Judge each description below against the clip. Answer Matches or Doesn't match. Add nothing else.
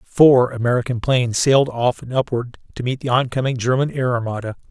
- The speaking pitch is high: Doesn't match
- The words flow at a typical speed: Matches